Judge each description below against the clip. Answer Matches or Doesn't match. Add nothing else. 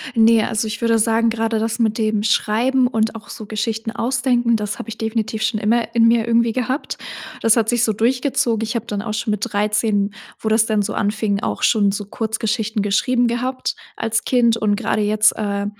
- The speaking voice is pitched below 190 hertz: Doesn't match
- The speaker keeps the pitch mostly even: Matches